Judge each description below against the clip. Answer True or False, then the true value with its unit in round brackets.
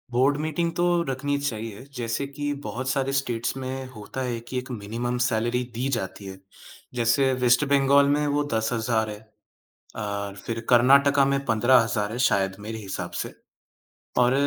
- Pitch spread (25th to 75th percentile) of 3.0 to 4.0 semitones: True (3.4 semitones)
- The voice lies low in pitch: True (125 Hz)